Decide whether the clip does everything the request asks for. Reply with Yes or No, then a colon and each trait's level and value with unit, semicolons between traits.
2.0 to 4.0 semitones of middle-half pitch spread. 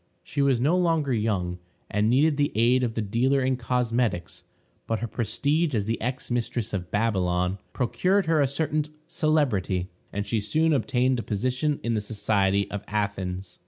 No: wide, 5.4 semitones